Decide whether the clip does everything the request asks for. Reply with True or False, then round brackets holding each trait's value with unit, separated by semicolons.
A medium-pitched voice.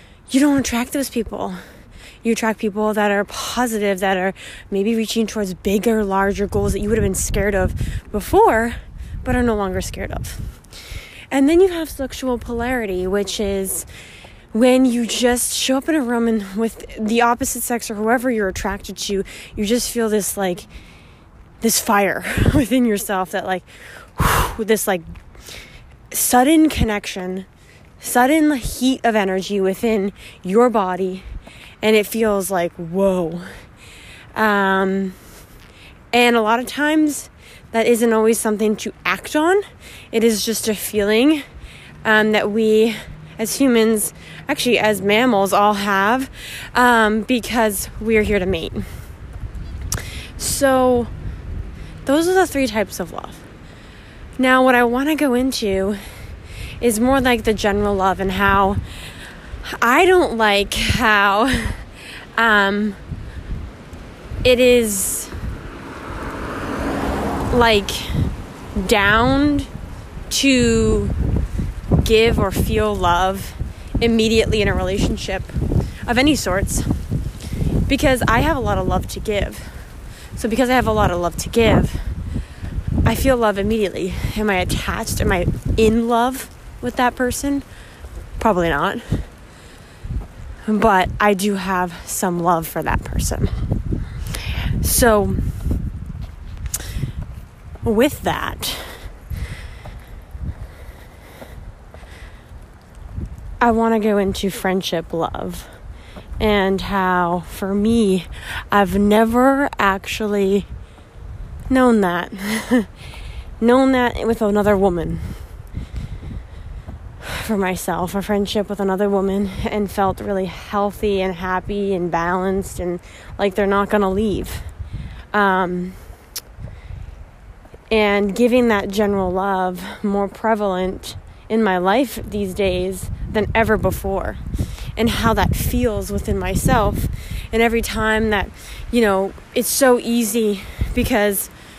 False (205 Hz)